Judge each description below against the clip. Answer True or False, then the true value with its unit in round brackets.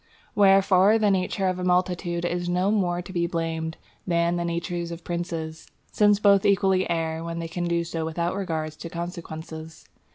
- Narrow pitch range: True (1.9 semitones)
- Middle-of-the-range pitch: True (175 Hz)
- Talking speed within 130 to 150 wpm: False (175 wpm)